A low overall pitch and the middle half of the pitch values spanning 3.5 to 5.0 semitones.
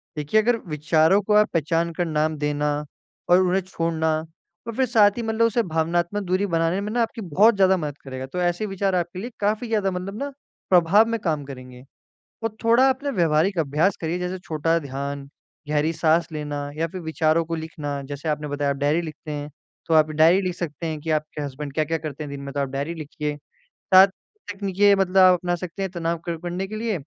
No: medium, 165 Hz; average, 4.2 semitones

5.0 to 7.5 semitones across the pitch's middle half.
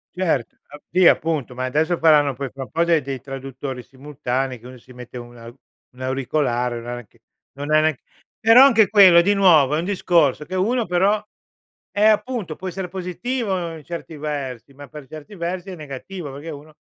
Yes: wide, 5.4 semitones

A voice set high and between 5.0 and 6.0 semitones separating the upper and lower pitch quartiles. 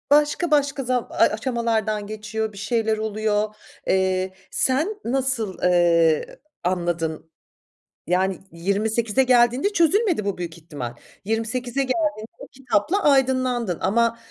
Yes: high, 220 Hz; wide, 5.4 semitones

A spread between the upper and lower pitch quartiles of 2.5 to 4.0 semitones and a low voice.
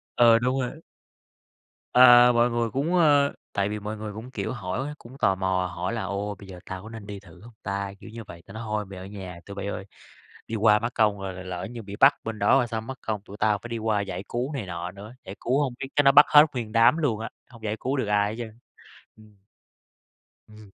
Yes: average, 3.3 semitones; low, 110 Hz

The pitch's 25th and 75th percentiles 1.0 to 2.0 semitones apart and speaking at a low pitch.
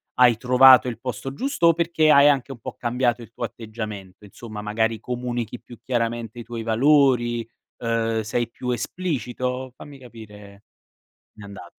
No: narrow, 2.4 semitones; low, 120 Hz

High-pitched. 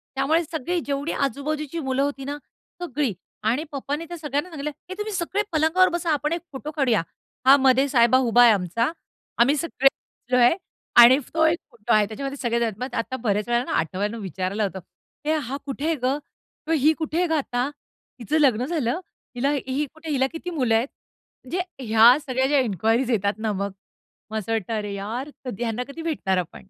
Yes: very high, 265 Hz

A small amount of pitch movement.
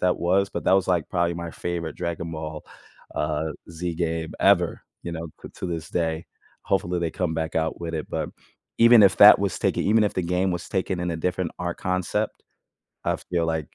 Yes: narrow, 1.9 semitones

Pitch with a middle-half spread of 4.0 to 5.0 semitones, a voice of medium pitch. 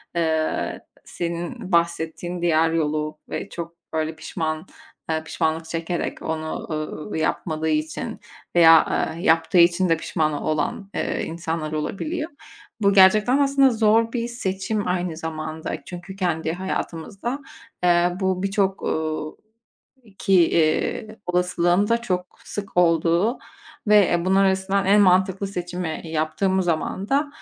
No: average, 3.3 semitones; medium, 175 Hz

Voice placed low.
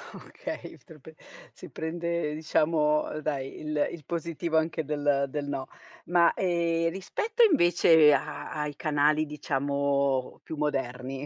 No: medium, 150 Hz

